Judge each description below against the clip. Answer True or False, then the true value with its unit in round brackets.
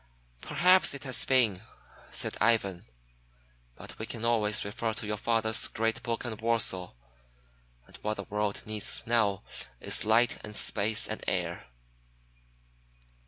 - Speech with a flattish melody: True (2.0 semitones)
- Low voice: True (110 Hz)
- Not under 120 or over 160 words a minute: True (135 wpm)